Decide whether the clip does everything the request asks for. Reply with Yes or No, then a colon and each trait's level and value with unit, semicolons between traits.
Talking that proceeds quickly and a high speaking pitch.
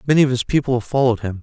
No: fast, 295 wpm; low, 125 Hz